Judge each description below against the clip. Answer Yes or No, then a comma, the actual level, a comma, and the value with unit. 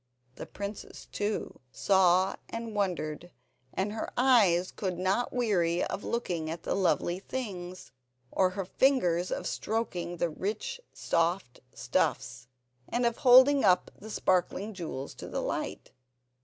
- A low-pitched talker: No, medium, 185 Hz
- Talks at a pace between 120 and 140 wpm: Yes, slow, 135 wpm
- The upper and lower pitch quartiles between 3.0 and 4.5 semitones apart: Yes, average, 3.9 semitones